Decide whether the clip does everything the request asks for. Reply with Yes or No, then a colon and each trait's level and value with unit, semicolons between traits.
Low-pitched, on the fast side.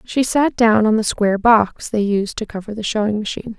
No: high, 215 Hz; fast, 235 wpm